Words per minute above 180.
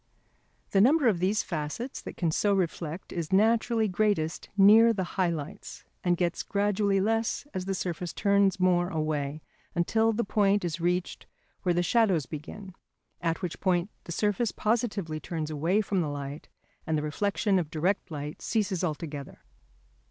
No: average, 160 wpm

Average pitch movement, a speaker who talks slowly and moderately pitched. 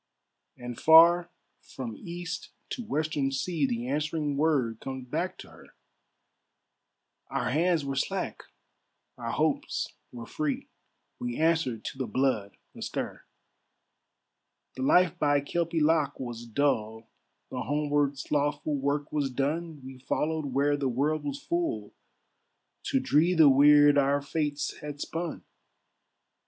Yes: average, 3.2 semitones; slow, 125 wpm; medium, 145 Hz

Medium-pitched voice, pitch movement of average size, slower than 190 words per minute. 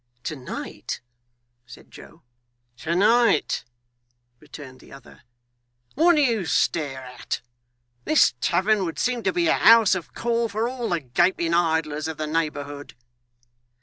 No: medium, 170 Hz; wide, 7.2 semitones; average, 140 wpm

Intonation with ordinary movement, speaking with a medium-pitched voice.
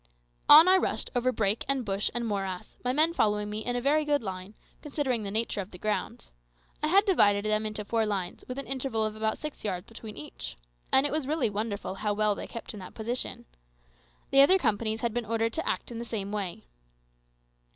No: average, 4.2 semitones; high, 220 Hz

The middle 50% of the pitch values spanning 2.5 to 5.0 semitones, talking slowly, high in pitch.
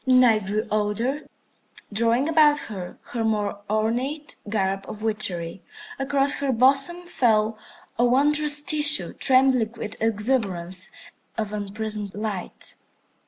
Yes: average, 4.6 semitones; slow, 115 wpm; high, 225 Hz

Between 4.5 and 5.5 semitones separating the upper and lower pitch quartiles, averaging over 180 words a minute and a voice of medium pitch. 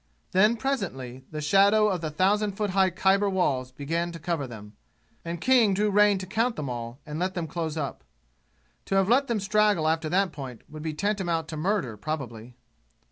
Yes: average, 5.2 semitones; average, 190 wpm; medium, 175 Hz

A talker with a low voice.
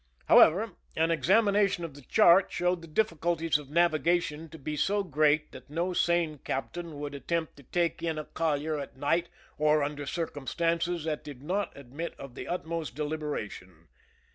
No: medium, 160 Hz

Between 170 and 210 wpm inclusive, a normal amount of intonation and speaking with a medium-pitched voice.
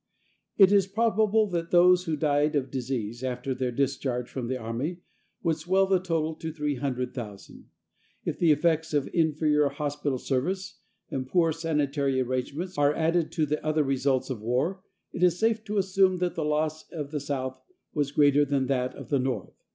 Yes: average, 175 wpm; average, 4.4 semitones; medium, 150 Hz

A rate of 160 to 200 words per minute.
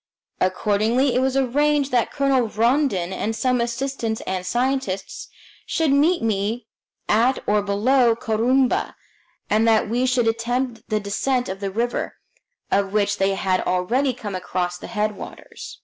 No: average, 145 wpm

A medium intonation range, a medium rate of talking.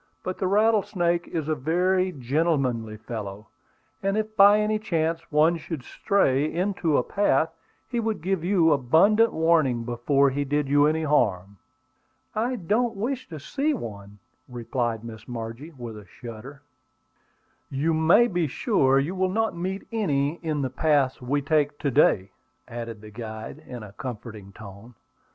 No: wide, 7.4 semitones; average, 155 wpm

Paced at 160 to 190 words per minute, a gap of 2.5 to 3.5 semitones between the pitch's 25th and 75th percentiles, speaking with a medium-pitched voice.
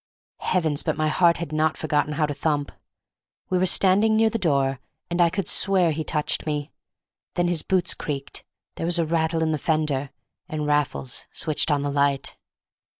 Yes: average, 180 wpm; average, 2.9 semitones; medium, 155 Hz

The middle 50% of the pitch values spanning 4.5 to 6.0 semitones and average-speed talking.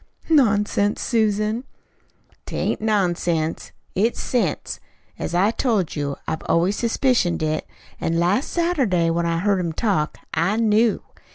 No: average, 5.0 semitones; slow, 130 wpm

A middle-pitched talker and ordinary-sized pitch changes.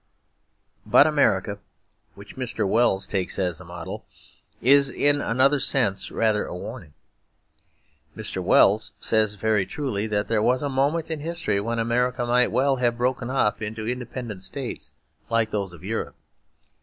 No: low, 115 Hz; average, 4.0 semitones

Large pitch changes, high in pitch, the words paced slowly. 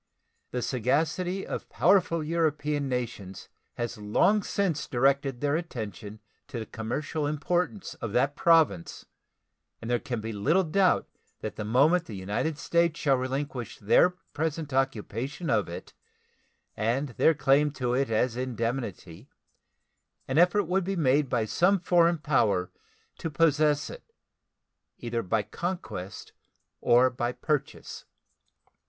No: wide, 5.7 semitones; low, 135 Hz; slow, 130 wpm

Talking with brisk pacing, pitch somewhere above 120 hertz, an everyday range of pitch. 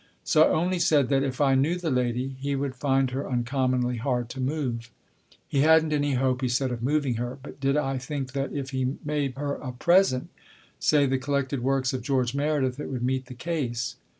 No: fast, 210 wpm; low, 135 Hz; narrow, 2.2 semitones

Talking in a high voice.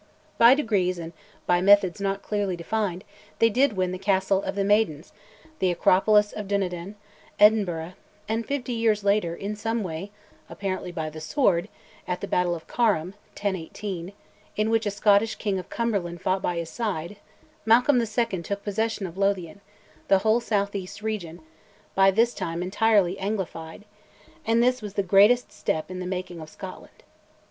Yes: high, 200 Hz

